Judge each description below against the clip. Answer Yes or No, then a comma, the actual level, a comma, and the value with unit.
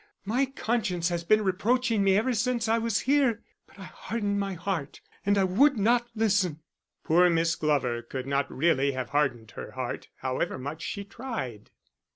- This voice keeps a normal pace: Yes, average, 170 wpm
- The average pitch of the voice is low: No, high, 195 Hz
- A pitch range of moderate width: No, wide, 7.4 semitones